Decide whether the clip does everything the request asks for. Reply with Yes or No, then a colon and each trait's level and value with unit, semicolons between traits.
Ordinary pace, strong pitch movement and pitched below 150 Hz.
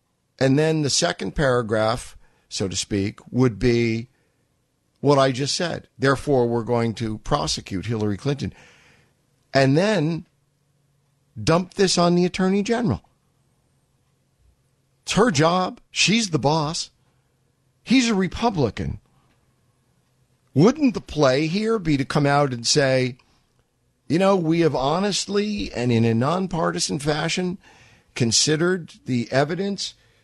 No: slow, 120 wpm; wide, 5.9 semitones; medium, 140 Hz